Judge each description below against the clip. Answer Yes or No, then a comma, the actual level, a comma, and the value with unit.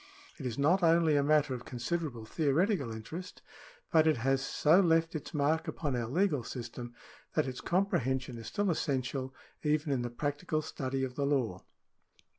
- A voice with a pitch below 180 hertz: Yes, medium, 140 Hz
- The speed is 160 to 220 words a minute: Yes, average, 170 wpm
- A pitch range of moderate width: Yes, average, 4.2 semitones